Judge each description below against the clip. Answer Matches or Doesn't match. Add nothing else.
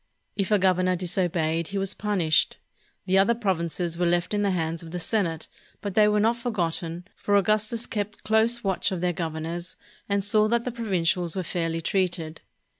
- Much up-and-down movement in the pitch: Doesn't match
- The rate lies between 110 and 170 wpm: Doesn't match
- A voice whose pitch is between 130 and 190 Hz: Matches